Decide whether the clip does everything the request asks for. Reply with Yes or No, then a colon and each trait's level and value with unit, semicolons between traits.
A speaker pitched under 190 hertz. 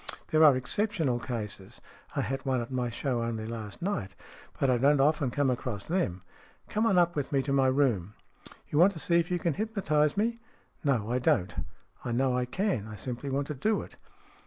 Yes: low, 135 Hz